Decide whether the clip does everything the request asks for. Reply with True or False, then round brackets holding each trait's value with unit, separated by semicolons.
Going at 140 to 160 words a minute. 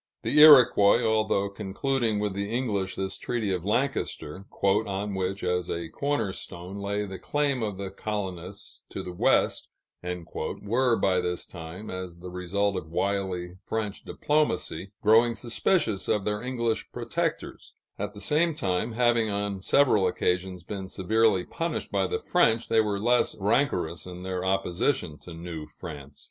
True (155 wpm)